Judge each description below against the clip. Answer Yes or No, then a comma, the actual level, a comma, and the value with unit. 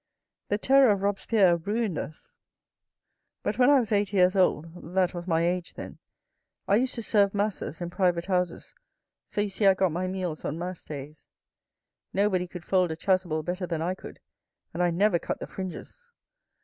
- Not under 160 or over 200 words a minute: Yes, average, 185 wpm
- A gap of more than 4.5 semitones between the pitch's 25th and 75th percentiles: No, average, 2.8 semitones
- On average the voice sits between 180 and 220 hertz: Yes, medium, 185 Hz